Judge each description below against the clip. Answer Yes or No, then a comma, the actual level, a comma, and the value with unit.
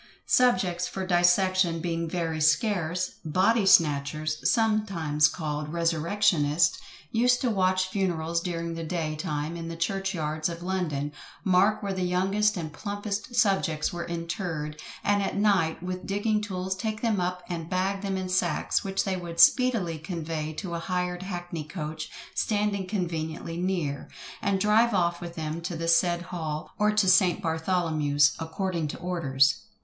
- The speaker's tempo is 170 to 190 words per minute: No, average, 155 wpm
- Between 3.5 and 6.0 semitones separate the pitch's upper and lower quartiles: No, average, 3.1 semitones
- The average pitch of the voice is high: No, medium, 175 Hz